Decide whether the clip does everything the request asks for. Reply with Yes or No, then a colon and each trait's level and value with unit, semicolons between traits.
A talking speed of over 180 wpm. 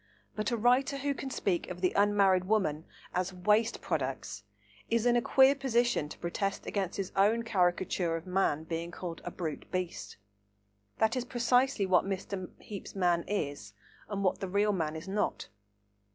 No: average, 170 wpm